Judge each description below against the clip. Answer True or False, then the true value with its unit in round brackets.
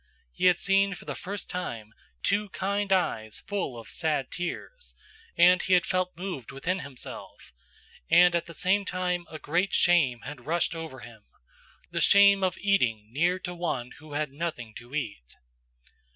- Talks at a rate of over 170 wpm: False (165 wpm)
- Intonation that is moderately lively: False (5.7 semitones)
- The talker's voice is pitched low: False (170 Hz)